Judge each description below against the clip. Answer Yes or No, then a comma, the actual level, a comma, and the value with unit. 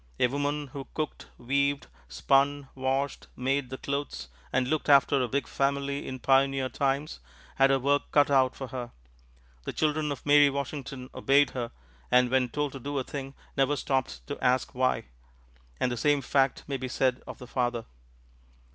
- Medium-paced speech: Yes, average, 175 wpm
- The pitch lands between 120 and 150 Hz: Yes, low, 135 Hz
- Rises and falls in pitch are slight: Yes, narrow, 1.8 semitones